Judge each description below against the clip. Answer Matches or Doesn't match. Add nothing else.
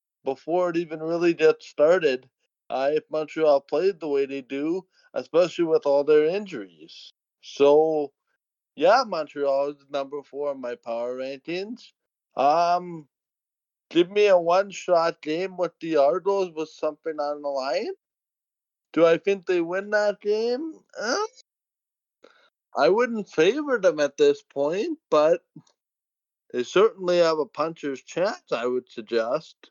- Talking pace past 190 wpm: Doesn't match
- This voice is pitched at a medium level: Matches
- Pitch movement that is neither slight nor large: Doesn't match